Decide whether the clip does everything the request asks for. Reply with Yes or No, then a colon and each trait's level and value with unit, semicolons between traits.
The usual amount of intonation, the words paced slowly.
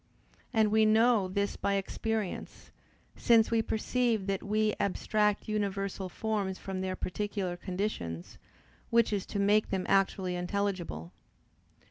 No: narrow, 2.3 semitones; slow, 125 wpm